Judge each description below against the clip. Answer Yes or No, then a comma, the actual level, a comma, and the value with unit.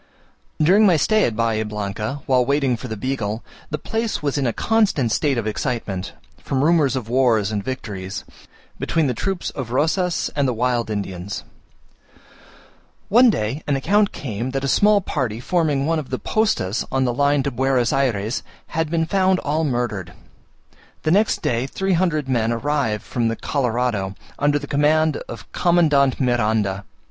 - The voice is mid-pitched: No, low, 130 Hz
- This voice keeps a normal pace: Yes, average, 170 wpm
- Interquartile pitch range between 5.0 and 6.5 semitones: Yes, wide, 5.4 semitones